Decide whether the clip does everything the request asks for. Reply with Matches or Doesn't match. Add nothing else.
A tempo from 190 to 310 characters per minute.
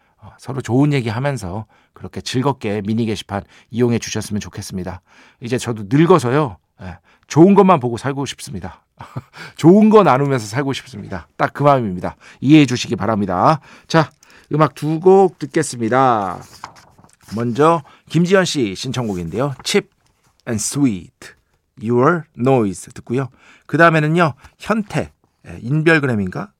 Doesn't match